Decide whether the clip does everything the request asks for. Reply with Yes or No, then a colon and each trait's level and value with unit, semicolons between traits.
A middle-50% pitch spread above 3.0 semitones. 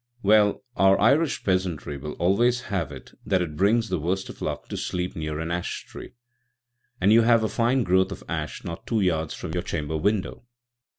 Yes: average, 4.2 semitones